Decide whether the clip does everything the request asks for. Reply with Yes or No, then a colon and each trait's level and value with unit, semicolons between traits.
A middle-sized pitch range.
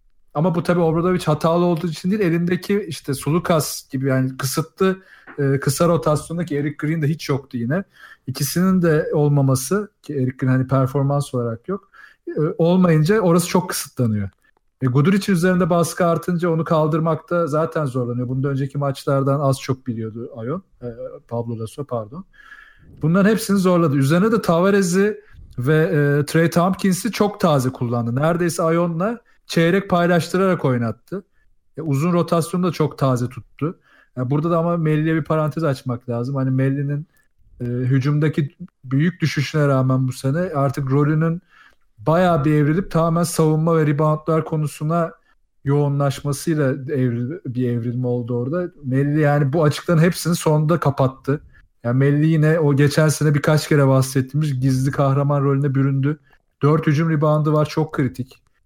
Yes: average, 4.0 semitones